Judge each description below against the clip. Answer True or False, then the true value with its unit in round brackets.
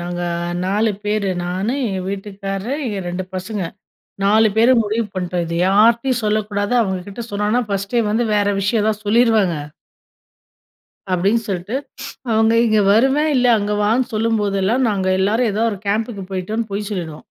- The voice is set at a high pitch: True (210 Hz)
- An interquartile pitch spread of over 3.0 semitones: False (2.7 semitones)